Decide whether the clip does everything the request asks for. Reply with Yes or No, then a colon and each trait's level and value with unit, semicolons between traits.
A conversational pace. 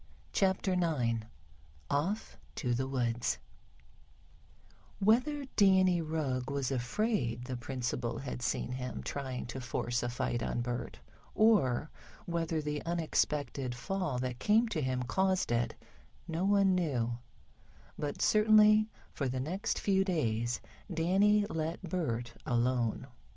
No: slow, 125 wpm